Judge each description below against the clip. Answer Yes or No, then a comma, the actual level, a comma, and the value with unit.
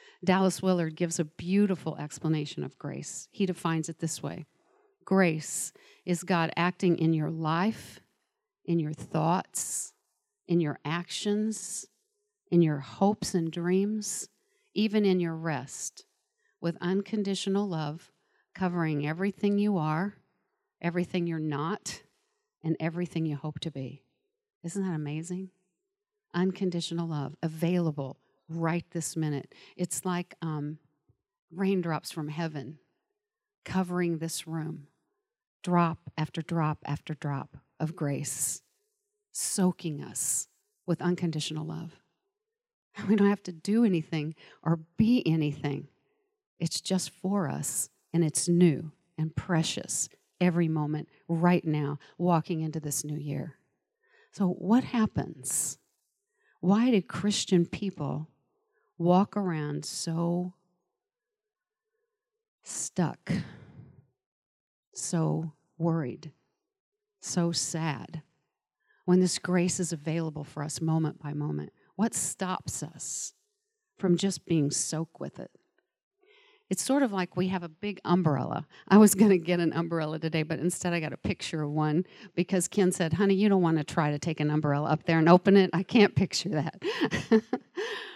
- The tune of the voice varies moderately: Yes, average, 4.0 semitones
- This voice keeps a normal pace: No, slow, 130 wpm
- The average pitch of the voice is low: No, medium, 175 Hz